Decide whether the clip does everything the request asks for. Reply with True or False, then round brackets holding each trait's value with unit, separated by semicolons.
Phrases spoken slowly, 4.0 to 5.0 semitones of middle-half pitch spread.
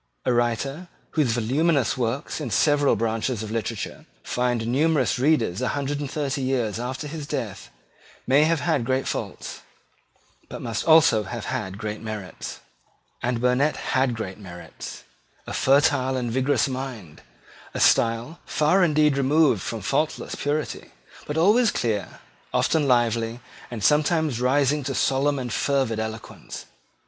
False (145 wpm; 4.3 semitones)